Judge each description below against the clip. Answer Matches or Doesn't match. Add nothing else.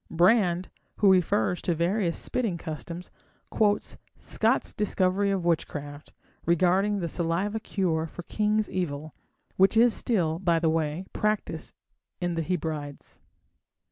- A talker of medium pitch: Matches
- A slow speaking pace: Matches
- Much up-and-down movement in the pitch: Doesn't match